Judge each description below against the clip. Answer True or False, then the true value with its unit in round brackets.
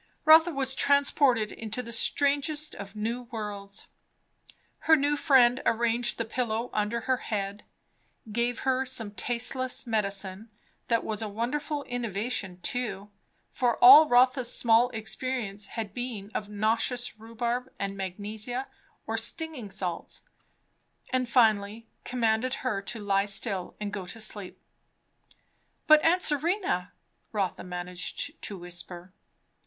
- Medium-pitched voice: False (230 Hz)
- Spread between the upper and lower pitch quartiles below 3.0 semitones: False (3.9 semitones)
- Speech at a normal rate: False (125 wpm)